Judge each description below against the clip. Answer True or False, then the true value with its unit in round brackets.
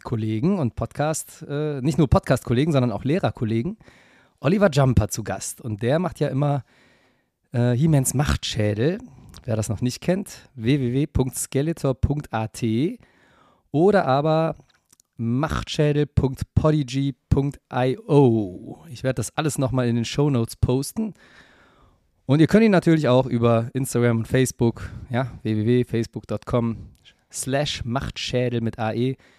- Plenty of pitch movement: False (3.8 semitones)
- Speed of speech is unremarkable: False (115 wpm)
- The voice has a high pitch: False (130 Hz)